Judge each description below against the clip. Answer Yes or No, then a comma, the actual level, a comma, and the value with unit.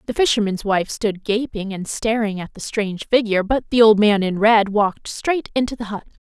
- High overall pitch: Yes, high, 215 Hz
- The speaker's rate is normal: No, fast, 210 wpm